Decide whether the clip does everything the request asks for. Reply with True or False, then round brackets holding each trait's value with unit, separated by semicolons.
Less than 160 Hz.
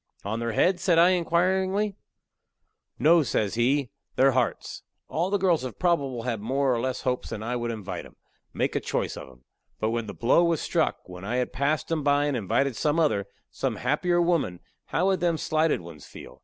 True (140 Hz)